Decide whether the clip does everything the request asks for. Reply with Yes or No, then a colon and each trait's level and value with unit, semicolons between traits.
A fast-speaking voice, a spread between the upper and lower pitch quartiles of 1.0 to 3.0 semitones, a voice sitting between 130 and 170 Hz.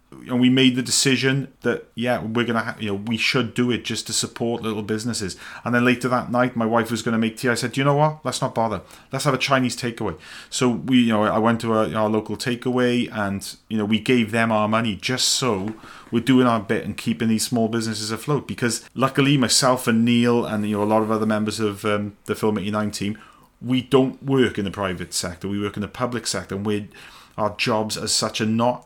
No: fast, 250 wpm; average, 2.7 semitones; low, 115 Hz